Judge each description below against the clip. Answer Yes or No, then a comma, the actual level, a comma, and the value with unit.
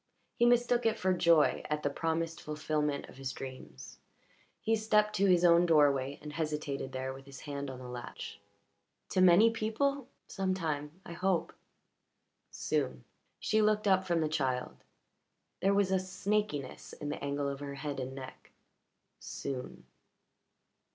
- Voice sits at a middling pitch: Yes, medium, 160 Hz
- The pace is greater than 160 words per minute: No, average, 155 wpm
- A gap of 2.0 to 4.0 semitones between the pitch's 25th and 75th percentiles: No, wide, 5.5 semitones